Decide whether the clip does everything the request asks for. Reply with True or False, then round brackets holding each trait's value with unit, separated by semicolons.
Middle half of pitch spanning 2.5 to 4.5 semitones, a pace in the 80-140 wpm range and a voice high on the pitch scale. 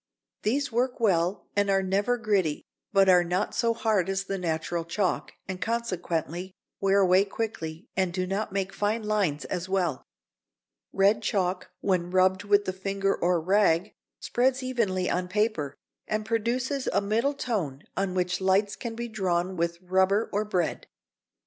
False (2.9 semitones; 160 wpm; 195 Hz)